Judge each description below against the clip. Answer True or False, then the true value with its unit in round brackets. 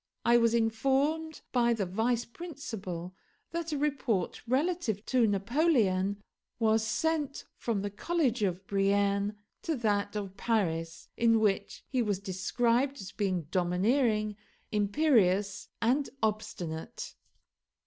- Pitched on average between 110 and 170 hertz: False (220 Hz)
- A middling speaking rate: False (120 wpm)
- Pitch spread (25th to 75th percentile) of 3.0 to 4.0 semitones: False (4.6 semitones)